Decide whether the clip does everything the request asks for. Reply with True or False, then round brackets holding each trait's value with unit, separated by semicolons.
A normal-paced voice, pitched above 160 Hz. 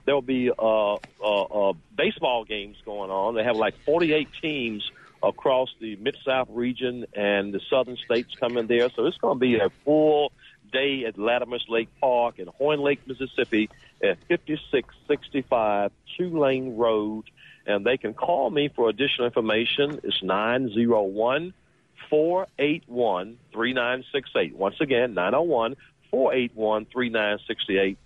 False (175 wpm; 120 Hz)